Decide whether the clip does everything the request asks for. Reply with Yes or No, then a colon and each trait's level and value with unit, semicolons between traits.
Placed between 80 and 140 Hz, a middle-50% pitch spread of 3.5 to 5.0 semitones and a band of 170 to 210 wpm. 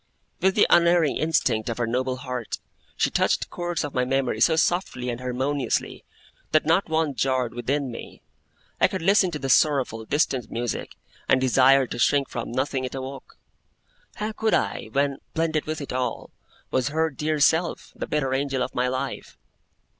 Yes: low, 135 Hz; average, 3.8 semitones; average, 175 wpm